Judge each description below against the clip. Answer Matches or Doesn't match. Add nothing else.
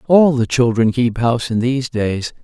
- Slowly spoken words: Doesn't match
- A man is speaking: Matches